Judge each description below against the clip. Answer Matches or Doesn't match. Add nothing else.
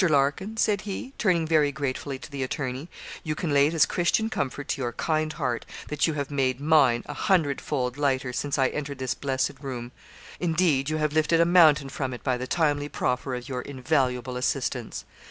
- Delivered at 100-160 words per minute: Doesn't match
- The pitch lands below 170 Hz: Matches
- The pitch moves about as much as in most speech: Matches